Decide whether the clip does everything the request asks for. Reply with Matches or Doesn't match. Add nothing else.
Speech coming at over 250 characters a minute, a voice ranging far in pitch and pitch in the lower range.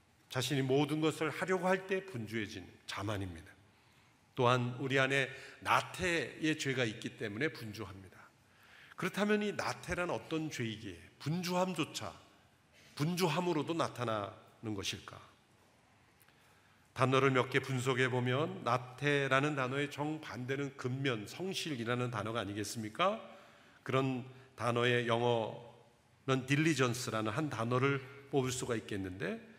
Doesn't match